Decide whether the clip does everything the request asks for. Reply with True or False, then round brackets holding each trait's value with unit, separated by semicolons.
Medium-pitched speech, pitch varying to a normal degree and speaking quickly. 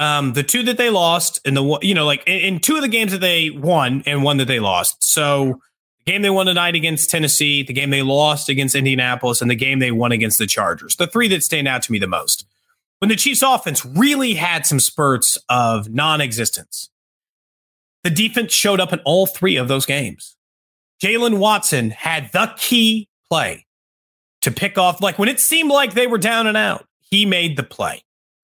False (160 Hz; 6.8 semitones; 210 wpm)